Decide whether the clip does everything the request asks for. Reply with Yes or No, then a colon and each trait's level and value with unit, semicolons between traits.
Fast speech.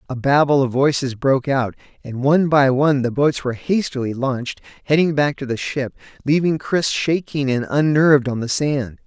No: average, 185 wpm